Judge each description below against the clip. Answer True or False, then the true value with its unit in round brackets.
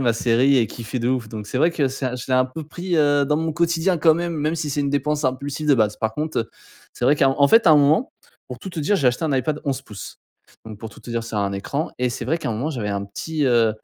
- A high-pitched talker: False (140 Hz)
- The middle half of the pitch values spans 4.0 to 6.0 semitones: True (4.7 semitones)